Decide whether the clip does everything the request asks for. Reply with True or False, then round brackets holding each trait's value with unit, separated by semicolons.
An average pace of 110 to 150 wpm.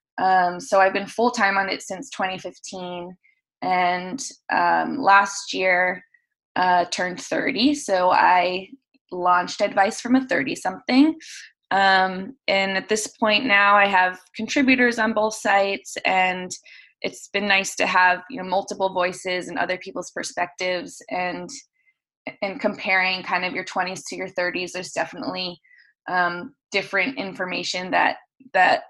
True (140 wpm)